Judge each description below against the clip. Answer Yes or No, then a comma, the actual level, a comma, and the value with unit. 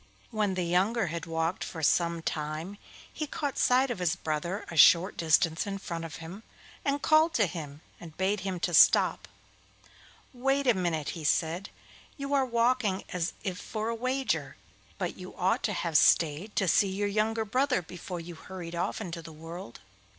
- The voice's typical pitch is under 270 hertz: Yes, medium, 185 Hz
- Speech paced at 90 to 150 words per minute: No, average, 180 wpm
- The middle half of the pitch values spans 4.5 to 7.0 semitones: Yes, average, 5.1 semitones